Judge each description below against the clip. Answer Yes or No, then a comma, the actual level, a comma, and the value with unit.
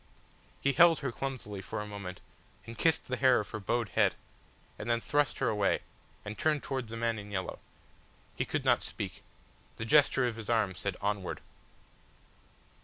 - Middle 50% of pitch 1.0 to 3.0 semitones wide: No, average, 4.3 semitones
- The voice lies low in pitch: Yes, low, 115 Hz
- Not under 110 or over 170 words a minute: No, average, 180 wpm